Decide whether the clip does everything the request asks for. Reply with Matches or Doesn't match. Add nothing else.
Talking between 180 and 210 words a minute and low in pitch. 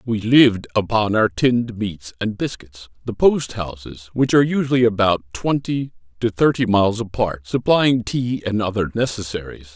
Doesn't match